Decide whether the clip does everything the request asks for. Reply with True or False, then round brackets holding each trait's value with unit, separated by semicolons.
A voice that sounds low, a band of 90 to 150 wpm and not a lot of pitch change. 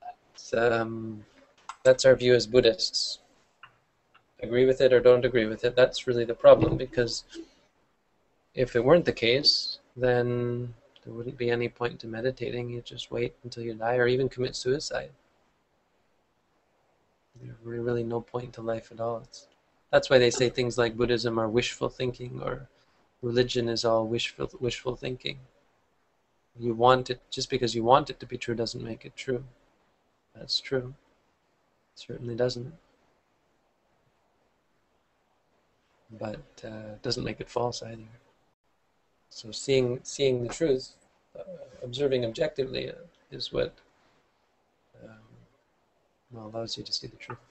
True (120 Hz; 145 wpm; 1.5 semitones)